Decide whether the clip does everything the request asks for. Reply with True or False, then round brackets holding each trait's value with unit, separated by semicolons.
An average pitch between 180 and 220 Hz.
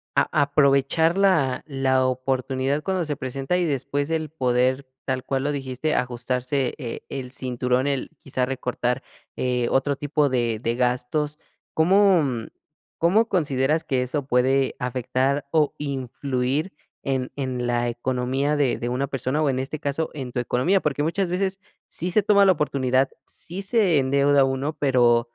False (135 Hz)